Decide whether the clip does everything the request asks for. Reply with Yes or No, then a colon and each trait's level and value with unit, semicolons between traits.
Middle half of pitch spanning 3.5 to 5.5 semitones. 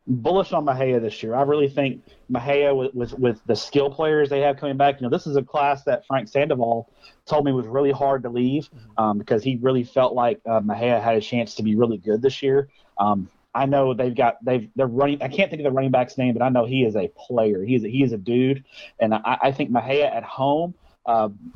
No: average, 3.0 semitones